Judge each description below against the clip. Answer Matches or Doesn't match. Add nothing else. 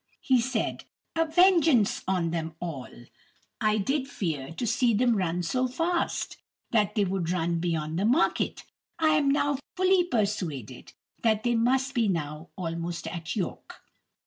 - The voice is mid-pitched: Doesn't match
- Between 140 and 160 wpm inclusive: Matches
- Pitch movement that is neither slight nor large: Doesn't match